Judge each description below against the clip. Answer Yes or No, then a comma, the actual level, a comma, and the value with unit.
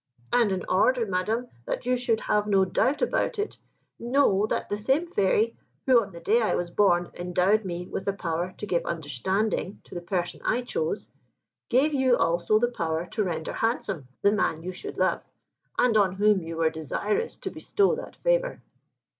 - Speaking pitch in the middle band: No, high, 205 Hz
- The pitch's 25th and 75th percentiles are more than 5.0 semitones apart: Yes, wide, 5.6 semitones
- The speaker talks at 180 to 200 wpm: Yes, average, 190 wpm